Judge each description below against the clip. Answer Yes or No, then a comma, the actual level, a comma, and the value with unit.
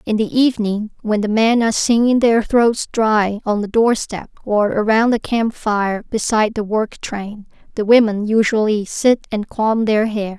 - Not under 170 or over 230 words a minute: Yes, average, 180 wpm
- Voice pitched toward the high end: Yes, high, 220 Hz